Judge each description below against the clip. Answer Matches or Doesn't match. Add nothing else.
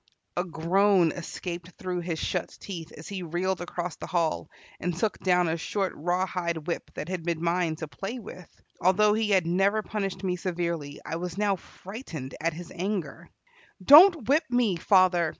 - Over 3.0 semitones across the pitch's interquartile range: Doesn't match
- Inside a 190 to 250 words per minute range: Doesn't match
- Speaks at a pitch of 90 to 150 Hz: Doesn't match